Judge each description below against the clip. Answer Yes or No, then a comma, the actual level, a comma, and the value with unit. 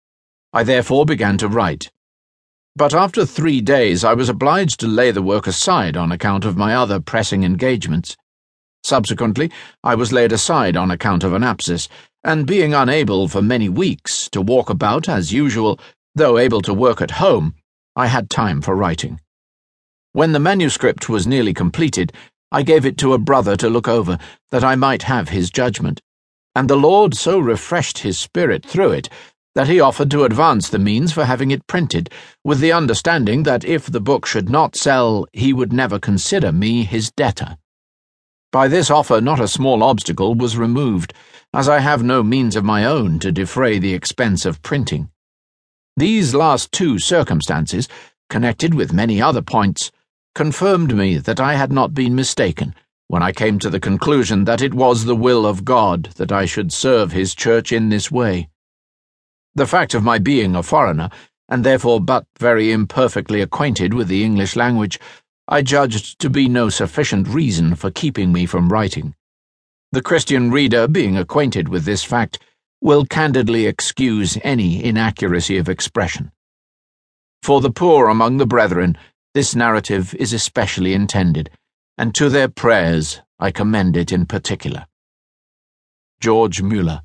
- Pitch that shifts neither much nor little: No, wide, 6.1 semitones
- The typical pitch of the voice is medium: No, low, 110 Hz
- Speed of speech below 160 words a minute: No, average, 165 wpm